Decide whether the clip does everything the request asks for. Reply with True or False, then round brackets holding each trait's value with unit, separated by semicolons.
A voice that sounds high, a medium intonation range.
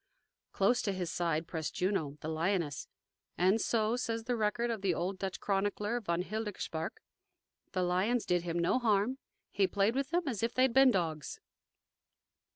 True (195 Hz; 4.7 semitones)